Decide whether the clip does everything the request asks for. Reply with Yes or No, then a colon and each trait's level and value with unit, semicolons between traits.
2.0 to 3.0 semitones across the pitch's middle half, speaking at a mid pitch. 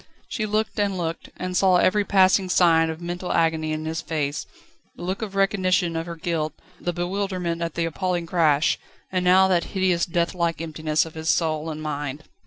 Yes: narrow, 2.5 semitones; medium, 170 Hz